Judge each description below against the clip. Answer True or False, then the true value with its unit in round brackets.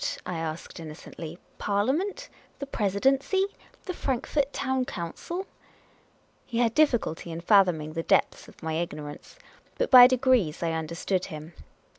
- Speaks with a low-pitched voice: False (200 Hz)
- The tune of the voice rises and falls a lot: True (8.4 semitones)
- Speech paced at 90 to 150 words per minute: True (135 wpm)